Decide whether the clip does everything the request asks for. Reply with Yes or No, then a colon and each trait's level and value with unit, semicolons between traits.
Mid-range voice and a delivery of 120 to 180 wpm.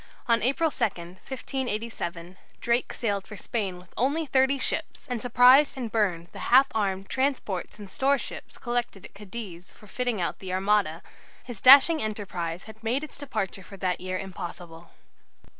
No: high, 215 Hz; average, 160 wpm